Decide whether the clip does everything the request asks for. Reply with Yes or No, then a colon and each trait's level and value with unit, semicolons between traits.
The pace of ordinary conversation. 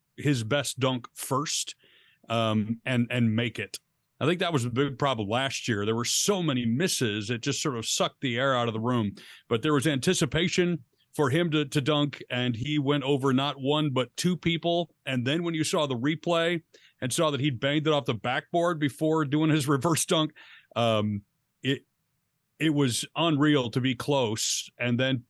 Yes: average, 195 wpm